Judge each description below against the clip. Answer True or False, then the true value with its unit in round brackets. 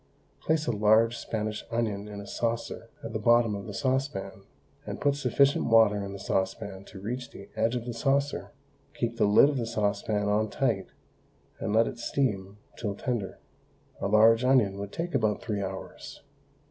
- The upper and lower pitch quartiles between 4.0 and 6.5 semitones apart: False (3.1 semitones)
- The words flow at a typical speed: True (180 wpm)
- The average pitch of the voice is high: False (110 Hz)